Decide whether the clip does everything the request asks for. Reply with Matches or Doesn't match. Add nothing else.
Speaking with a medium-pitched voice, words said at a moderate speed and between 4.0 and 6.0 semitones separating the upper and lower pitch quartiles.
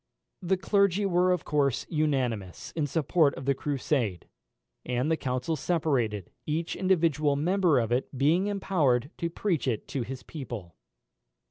Matches